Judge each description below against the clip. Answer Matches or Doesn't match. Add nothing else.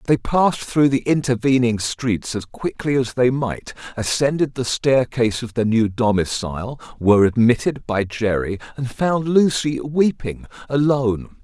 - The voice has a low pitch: Matches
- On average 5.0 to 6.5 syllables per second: Doesn't match